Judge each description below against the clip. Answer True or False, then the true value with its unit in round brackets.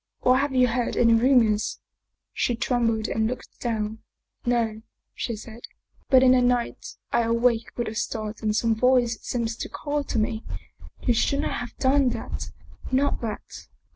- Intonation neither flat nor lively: False (2.2 semitones)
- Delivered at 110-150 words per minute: False (190 wpm)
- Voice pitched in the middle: False (235 Hz)